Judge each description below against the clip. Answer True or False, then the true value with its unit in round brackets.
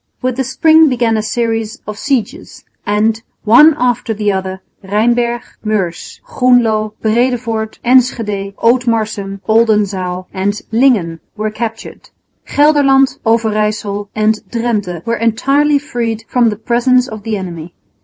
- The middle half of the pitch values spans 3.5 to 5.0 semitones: False (2.8 semitones)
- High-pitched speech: True (225 Hz)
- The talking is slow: True (125 wpm)